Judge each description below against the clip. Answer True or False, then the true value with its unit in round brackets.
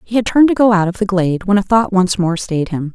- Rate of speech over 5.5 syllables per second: True (6.3 syllables/s)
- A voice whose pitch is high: True (195 Hz)